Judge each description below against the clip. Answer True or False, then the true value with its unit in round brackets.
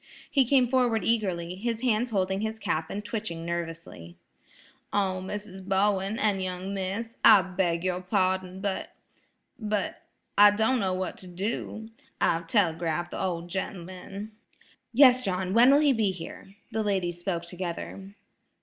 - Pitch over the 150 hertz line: True (190 Hz)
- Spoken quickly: False (140 wpm)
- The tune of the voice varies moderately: True (3.3 semitones)